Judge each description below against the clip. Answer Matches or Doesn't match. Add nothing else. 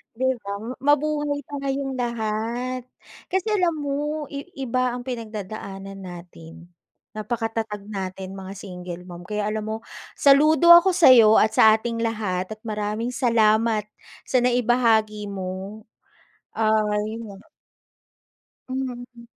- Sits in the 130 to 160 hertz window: Doesn't match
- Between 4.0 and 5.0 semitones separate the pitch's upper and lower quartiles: Doesn't match